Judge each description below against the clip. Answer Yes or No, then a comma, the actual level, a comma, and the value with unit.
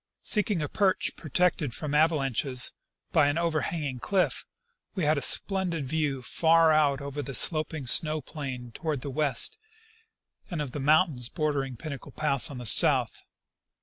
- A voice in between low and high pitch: Yes, medium, 150 Hz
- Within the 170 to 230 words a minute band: No, average, 155 wpm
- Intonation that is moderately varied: Yes, average, 3.1 semitones